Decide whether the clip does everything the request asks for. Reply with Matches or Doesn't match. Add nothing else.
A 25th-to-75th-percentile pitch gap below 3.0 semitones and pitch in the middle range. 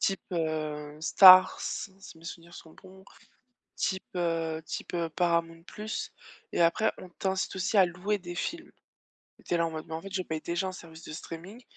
Matches